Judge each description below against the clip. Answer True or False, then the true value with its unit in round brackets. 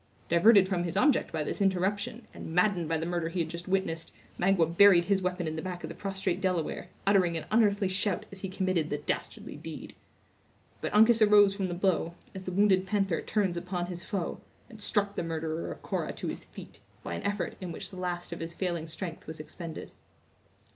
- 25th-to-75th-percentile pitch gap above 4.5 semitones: False (2.7 semitones)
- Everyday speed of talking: False (210 wpm)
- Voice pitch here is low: False (185 Hz)